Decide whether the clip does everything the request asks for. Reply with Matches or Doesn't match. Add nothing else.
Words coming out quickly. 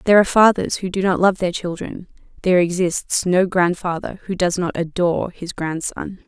Doesn't match